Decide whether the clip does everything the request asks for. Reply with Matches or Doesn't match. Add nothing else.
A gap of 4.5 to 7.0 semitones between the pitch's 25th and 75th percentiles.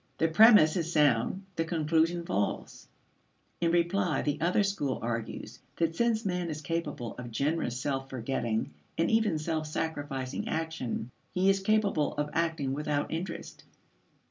Doesn't match